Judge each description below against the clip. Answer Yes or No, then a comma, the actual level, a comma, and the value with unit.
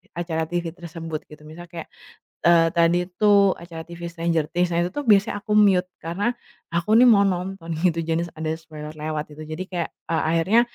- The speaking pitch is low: No, medium, 170 Hz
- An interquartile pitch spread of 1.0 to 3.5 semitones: Yes, narrow, 2.4 semitones